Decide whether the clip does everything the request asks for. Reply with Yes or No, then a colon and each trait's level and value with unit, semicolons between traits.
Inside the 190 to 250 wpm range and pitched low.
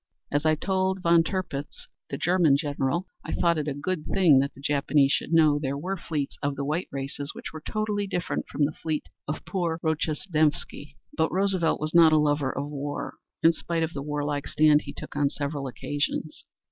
No: average, 195 wpm; medium, 155 Hz